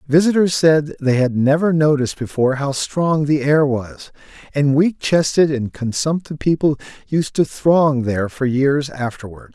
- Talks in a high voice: No, medium, 145 Hz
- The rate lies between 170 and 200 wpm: No, average, 155 wpm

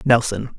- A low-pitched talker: Yes, low, 115 Hz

